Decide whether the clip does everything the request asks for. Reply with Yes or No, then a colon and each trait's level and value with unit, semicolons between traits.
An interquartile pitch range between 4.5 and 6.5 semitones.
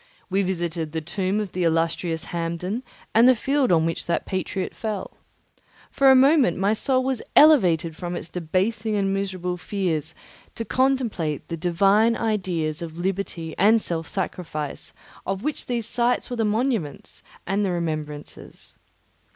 Yes: average, 5.1 semitones